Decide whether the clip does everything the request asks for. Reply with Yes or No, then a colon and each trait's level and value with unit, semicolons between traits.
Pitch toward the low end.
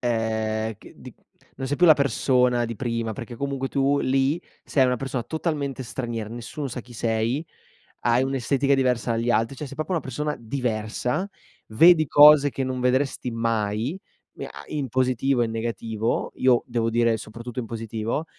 Yes: low, 125 Hz